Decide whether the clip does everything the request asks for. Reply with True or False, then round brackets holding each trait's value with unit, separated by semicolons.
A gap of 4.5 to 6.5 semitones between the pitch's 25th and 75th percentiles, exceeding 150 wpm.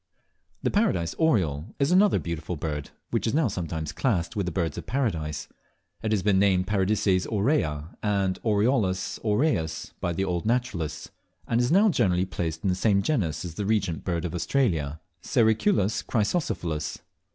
True (5.4 semitones; 165 wpm)